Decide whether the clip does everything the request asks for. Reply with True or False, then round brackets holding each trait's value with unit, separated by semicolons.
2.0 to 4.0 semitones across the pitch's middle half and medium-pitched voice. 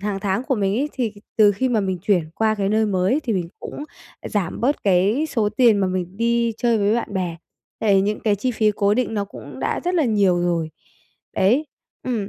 False (3.4 semitones; 210 Hz)